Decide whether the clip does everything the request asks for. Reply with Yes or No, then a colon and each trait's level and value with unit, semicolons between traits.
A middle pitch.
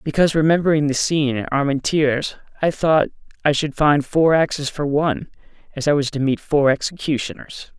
Yes: medium, 145 Hz